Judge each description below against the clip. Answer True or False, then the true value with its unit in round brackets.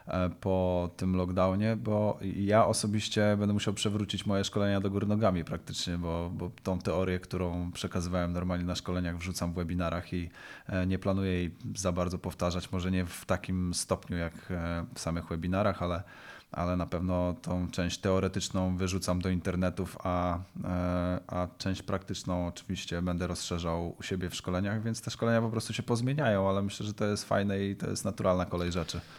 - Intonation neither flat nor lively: False (2.1 semitones)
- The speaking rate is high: True (170 wpm)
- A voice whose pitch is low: True (90 Hz)